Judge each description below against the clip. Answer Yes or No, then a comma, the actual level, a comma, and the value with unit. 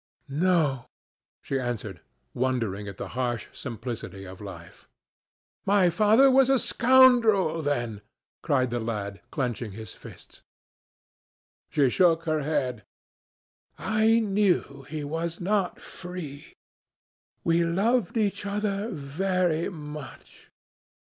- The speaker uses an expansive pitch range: Yes, wide, 8.3 semitones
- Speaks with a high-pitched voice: No, medium, 155 Hz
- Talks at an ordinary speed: No, slow, 110 wpm